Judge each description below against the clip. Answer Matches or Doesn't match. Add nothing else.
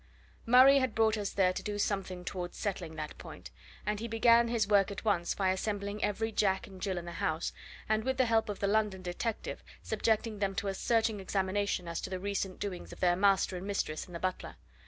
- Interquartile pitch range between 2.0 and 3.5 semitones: Matches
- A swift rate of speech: Matches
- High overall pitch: Matches